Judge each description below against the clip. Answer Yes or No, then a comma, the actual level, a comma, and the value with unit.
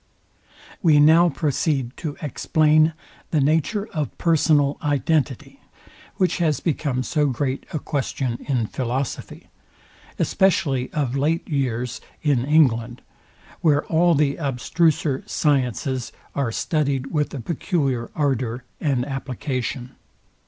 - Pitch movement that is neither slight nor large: Yes, average, 3.3 semitones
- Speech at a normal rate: No, slow, 110 wpm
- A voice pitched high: No, medium, 140 Hz